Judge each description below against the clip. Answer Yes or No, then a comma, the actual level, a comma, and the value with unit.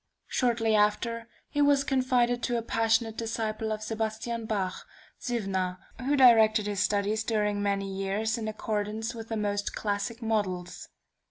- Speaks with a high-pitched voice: Yes, high, 220 Hz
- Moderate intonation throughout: No, narrow, 2.1 semitones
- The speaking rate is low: No, average, 145 wpm